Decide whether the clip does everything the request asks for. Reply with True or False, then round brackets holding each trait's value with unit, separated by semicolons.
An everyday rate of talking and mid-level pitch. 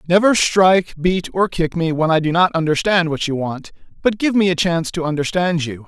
False (225 wpm; 170 Hz)